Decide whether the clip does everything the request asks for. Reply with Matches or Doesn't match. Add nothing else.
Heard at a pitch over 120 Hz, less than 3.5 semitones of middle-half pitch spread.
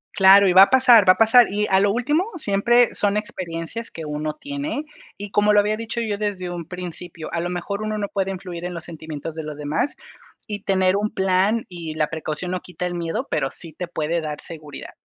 Doesn't match